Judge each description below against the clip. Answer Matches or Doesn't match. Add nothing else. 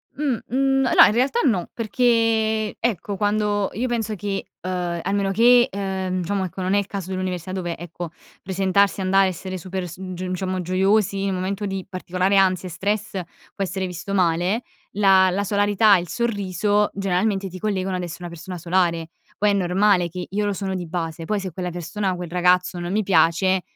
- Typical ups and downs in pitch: Doesn't match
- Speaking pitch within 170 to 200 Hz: Matches